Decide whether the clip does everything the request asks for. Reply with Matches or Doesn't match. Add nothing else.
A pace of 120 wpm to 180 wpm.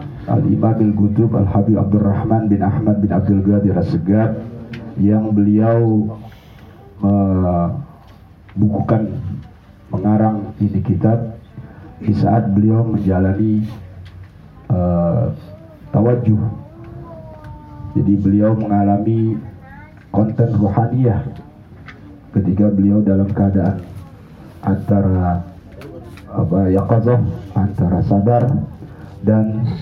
Doesn't match